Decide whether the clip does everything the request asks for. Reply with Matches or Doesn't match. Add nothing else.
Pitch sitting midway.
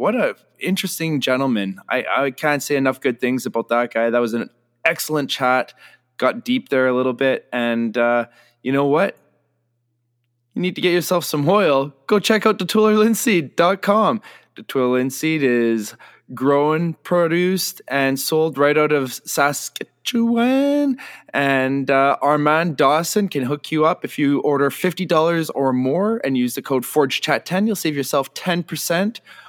Matches